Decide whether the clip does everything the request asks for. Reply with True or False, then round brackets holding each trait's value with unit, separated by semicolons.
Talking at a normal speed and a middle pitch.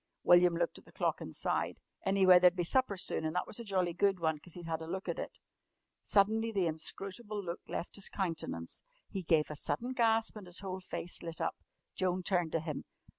False (220 wpm; 180 Hz)